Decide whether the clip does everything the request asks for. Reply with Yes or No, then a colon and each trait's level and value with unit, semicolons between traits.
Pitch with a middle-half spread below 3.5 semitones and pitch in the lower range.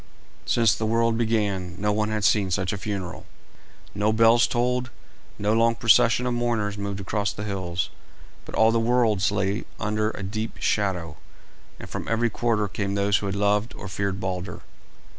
Yes: narrow, 2.4 semitones; low, 105 Hz